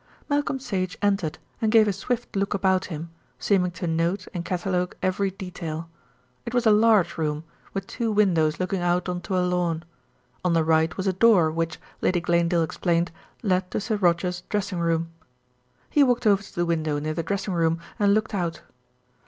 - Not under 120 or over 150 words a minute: No, average, 185 wpm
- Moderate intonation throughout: Yes, average, 3.1 semitones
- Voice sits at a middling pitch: Yes, medium, 180 Hz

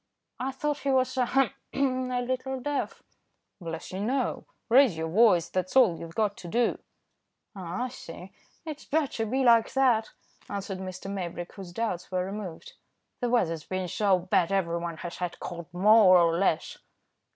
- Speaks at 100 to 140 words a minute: No, average, 165 wpm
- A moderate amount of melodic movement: No, wide, 6.3 semitones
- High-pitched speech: Yes, high, 200 Hz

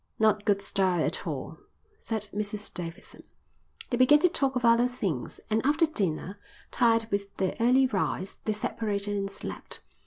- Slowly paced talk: No, average, 160 wpm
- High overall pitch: Yes, high, 210 Hz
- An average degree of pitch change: Yes, average, 3.5 semitones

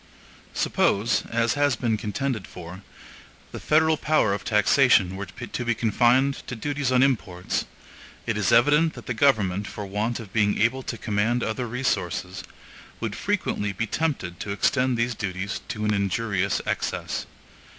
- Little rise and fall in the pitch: No, average, 4.1 semitones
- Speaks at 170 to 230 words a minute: No, average, 155 wpm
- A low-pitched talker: Yes, low, 115 Hz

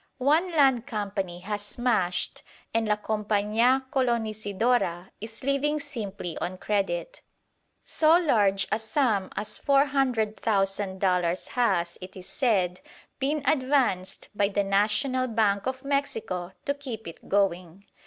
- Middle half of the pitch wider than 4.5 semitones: Yes, average, 5.0 semitones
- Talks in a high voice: Yes, high, 215 Hz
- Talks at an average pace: No, slow, 125 wpm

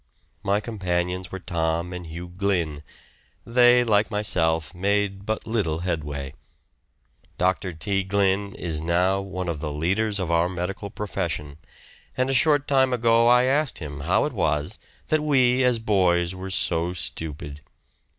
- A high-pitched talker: No, very low, 95 Hz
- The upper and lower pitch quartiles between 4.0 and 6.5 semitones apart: Yes, average, 4.5 semitones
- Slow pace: No, average, 150 wpm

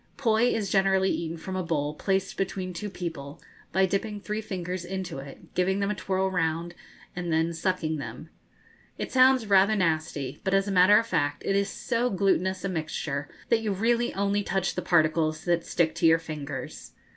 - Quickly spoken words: No, average, 190 wpm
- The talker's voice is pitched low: No, medium, 185 Hz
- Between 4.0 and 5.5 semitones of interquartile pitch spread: No, average, 3.4 semitones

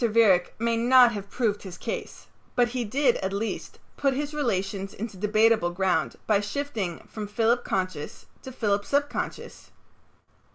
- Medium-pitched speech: No, high, 220 Hz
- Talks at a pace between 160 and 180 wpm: No, average, 150 wpm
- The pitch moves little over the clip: No, average, 3.7 semitones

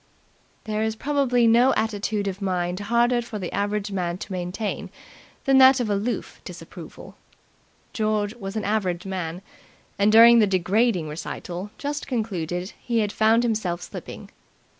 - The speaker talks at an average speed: Yes, average, 145 wpm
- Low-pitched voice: No, high, 210 Hz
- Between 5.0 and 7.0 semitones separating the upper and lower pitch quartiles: No, average, 3.8 semitones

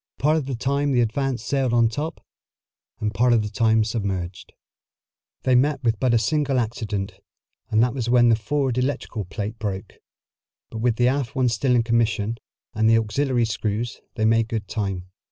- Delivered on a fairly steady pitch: No, average, 3.1 semitones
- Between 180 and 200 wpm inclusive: Yes, average, 190 wpm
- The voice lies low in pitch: Yes, low, 115 Hz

